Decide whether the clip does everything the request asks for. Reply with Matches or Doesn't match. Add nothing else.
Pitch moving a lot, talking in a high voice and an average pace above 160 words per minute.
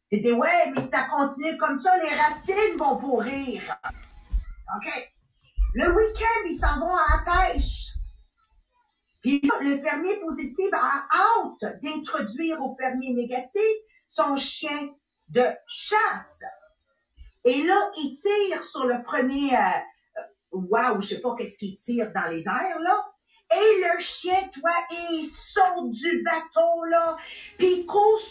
Doesn't match